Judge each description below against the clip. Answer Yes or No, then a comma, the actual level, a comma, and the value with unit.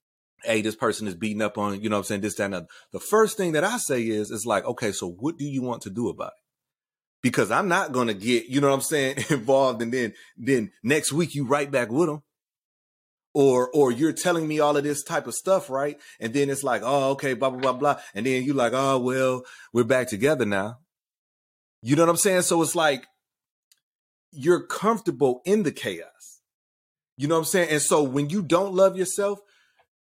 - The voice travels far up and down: Yes, wide, 5.9 semitones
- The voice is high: No, low, 135 Hz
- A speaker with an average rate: No, fast, 225 wpm